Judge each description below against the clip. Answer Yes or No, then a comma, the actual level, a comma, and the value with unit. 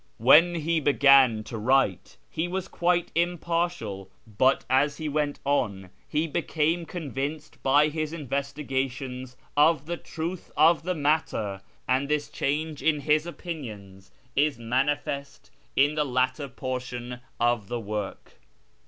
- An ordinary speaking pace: No, slow, 130 wpm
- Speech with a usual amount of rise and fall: Yes, average, 3.8 semitones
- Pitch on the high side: No, medium, 140 Hz